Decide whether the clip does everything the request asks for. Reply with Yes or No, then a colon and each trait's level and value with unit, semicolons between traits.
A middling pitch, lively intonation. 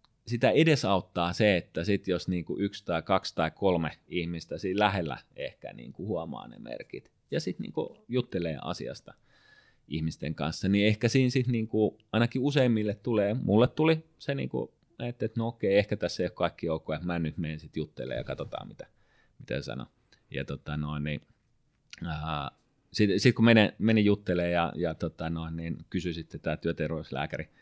No: very low, 95 Hz; wide, 6.0 semitones